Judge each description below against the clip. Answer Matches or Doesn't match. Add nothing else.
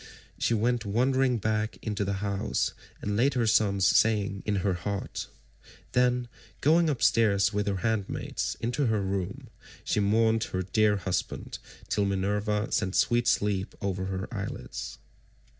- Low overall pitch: Matches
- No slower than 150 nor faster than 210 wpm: Doesn't match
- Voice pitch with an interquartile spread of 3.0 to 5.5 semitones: Doesn't match